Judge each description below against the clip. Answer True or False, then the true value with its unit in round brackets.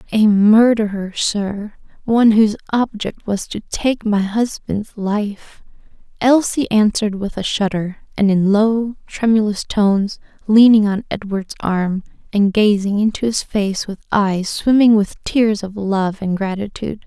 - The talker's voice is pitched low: False (210 Hz)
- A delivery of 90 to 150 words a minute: True (140 wpm)